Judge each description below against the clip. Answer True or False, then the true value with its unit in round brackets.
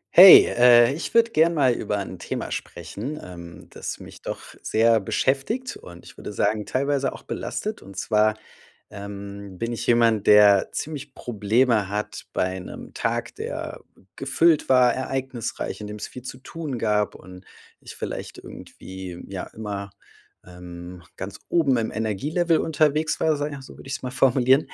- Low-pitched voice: True (115 Hz)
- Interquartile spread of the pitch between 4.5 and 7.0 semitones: True (5.5 semitones)